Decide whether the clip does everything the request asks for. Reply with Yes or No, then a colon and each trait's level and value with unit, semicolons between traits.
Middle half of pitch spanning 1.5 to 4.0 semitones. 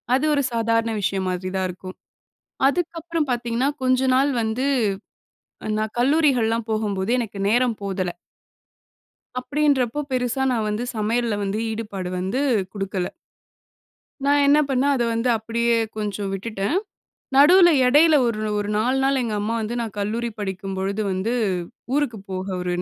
No: average, 4.4 semitones